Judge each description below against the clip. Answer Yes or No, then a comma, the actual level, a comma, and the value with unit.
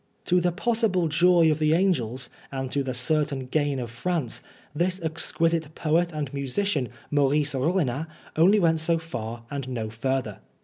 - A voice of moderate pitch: Yes, medium, 150 Hz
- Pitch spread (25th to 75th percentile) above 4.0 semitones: Yes, average, 4.4 semitones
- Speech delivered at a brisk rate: No, average, 160 wpm